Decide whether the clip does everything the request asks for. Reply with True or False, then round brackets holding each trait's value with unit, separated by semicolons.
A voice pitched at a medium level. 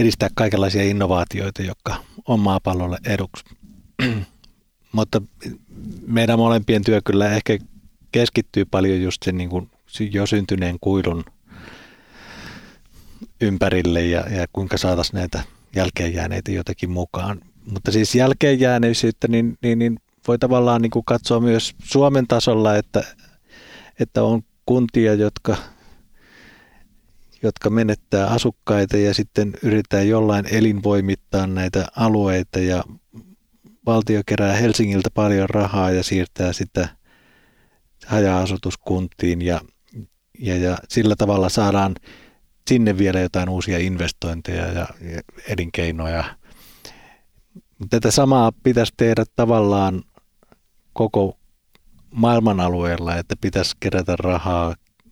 False (100 Hz)